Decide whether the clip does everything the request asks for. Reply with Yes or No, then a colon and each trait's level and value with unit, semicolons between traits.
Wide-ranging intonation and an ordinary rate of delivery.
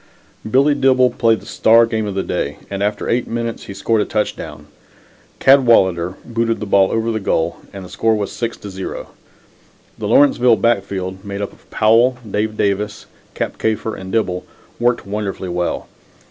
No: average, 3.0 semitones; average, 175 wpm